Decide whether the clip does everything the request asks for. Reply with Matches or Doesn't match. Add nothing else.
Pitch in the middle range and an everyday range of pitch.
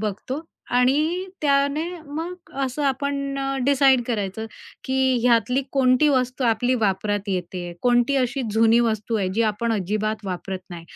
Doesn't match